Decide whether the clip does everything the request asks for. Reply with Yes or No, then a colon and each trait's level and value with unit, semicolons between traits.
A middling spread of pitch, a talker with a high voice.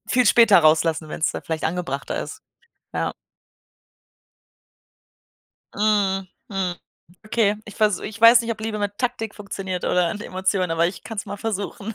Yes: average, 3.2 semitones; high, 200 Hz